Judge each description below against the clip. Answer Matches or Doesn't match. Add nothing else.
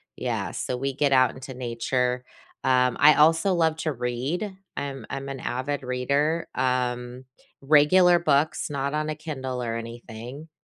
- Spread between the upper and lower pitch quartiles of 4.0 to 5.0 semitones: Doesn't match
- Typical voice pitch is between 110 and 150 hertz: Matches